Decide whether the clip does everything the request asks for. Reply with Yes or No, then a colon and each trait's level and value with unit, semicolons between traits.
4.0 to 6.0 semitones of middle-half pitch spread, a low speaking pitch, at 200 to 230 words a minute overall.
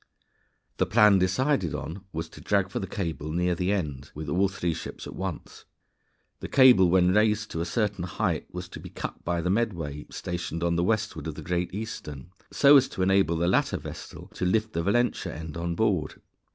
No: average, 3.6 semitones; very low, 90 Hz; fast, 205 wpm